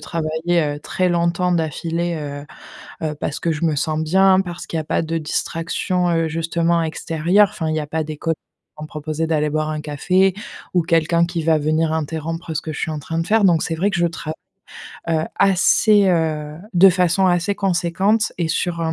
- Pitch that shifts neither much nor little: No, narrow, 2.1 semitones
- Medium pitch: Yes, medium, 165 Hz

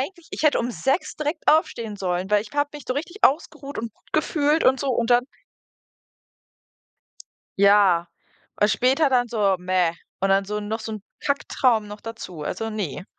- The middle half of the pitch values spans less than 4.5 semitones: No, wide, 5.8 semitones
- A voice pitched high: Yes, high, 225 Hz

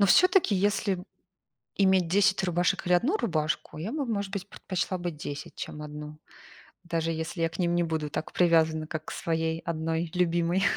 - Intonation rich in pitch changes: No, average, 2.9 semitones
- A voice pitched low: No, medium, 170 Hz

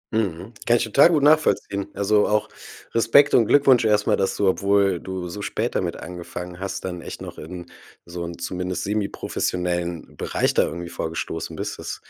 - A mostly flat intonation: No, average, 3.6 semitones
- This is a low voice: Yes, very low, 95 Hz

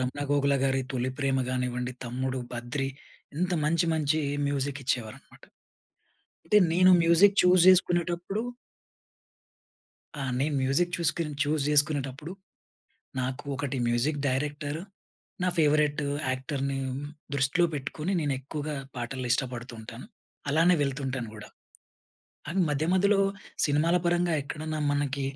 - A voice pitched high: No, medium, 145 Hz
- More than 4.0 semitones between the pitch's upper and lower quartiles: No, average, 3.7 semitones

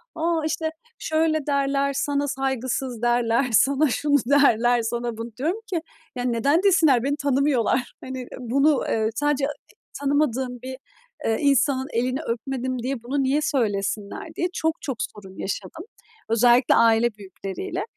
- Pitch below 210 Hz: No, very high, 260 Hz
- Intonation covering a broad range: No, average, 3.4 semitones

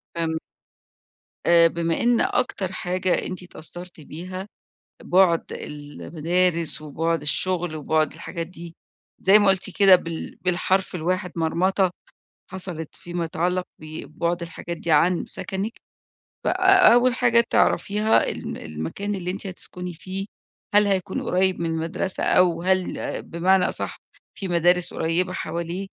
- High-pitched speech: No, medium, 180 Hz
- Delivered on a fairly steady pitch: Yes, narrow, 2.3 semitones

